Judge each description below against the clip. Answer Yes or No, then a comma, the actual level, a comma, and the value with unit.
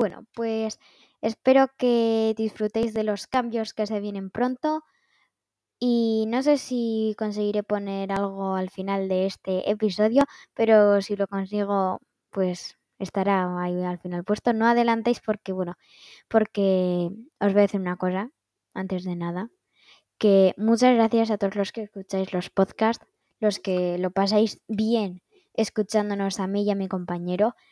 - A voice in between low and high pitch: No, high, 210 Hz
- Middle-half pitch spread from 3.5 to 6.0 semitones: No, average, 2.8 semitones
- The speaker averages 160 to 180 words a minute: No, average, 150 wpm